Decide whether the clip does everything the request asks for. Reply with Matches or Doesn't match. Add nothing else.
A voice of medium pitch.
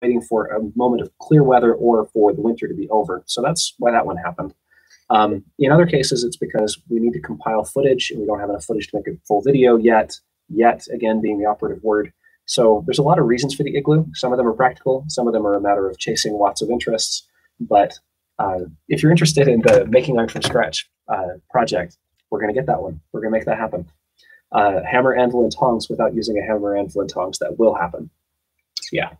Doesn't match